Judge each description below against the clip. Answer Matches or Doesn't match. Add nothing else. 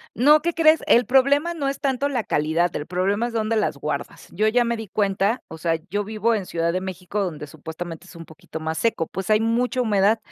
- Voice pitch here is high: Matches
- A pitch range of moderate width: Doesn't match